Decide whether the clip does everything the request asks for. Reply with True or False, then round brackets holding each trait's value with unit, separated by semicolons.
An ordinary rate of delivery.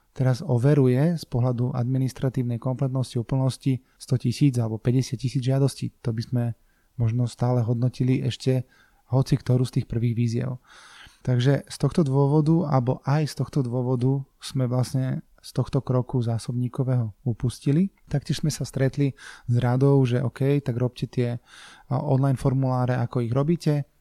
True (145 wpm)